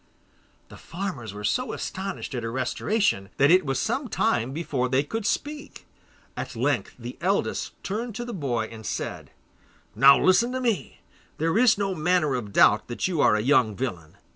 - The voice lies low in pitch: No, medium, 155 Hz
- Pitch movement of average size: No, wide, 9.0 semitones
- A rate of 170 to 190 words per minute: Yes, average, 180 wpm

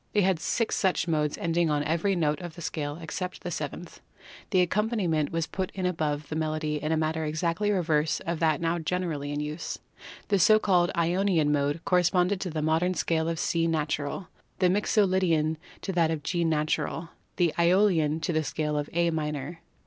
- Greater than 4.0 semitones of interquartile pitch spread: No, average, 2.7 semitones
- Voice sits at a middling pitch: Yes, medium, 165 Hz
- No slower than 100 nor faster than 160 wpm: No, average, 195 wpm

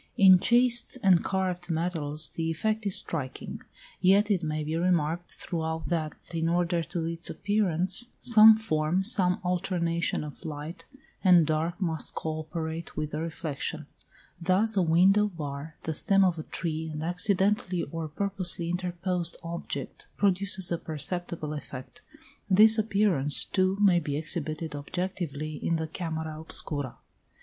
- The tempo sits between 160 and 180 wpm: No, average, 140 wpm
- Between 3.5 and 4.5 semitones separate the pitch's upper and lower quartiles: No, average, 3.1 semitones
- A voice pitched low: No, medium, 170 Hz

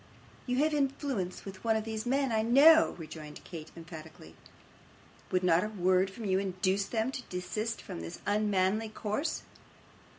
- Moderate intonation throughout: Yes, average, 4.1 semitones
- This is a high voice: Yes, high, 205 Hz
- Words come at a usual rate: Yes, average, 160 wpm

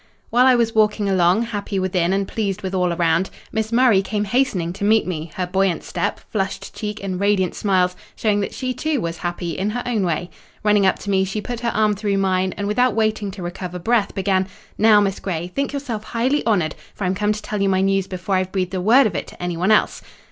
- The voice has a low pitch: No, high, 195 Hz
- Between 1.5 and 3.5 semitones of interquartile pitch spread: Yes, average, 2.8 semitones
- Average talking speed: No, fast, 230 wpm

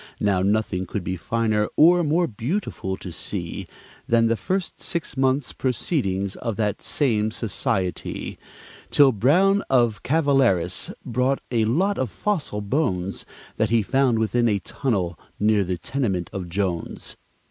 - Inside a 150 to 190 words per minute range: No, average, 140 wpm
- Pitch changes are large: Yes, wide, 5.7 semitones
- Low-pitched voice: Yes, low, 115 Hz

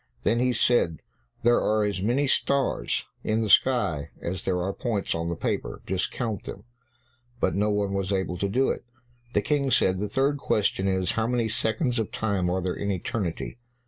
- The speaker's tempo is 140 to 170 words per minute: No, average, 195 wpm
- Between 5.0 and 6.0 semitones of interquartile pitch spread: No, average, 4.2 semitones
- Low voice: Yes, low, 105 Hz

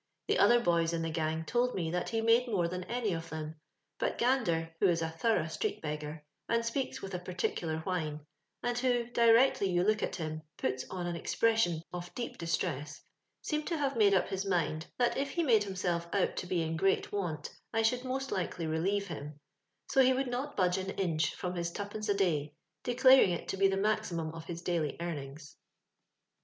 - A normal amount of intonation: No, wide, 5.8 semitones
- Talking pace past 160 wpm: Yes, fast, 205 wpm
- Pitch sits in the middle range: Yes, medium, 180 Hz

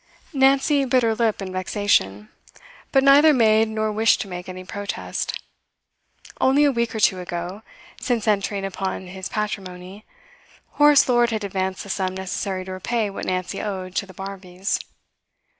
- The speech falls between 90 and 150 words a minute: No, average, 160 wpm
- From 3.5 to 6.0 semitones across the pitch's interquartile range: Yes, average, 3.8 semitones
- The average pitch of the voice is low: No, high, 200 Hz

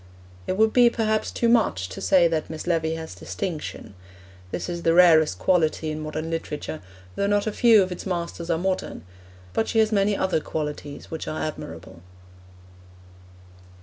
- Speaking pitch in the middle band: Yes, medium, 170 Hz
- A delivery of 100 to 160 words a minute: No, average, 170 wpm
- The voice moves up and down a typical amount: Yes, average, 4.3 semitones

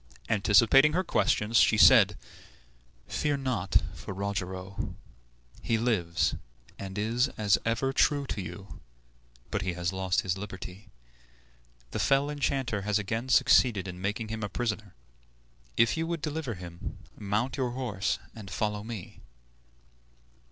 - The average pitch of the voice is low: Yes, low, 105 Hz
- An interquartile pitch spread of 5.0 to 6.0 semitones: No, average, 4.6 semitones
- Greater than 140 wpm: No, slow, 135 wpm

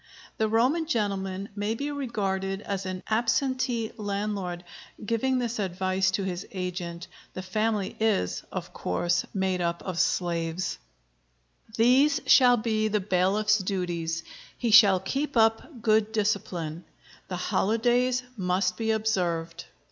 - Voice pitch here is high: Yes, high, 200 Hz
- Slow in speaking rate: Yes, slow, 125 wpm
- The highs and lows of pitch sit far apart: No, average, 3.6 semitones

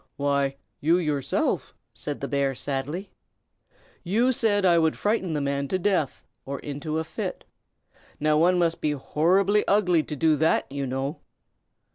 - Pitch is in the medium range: Yes, medium, 155 Hz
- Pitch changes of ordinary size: Yes, average, 4.4 semitones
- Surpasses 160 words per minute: No, average, 155 wpm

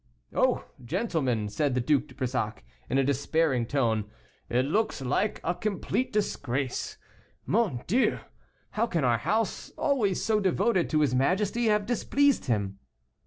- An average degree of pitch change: No, wide, 9.0 semitones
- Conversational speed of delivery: Yes, average, 145 wpm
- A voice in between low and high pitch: Yes, medium, 150 Hz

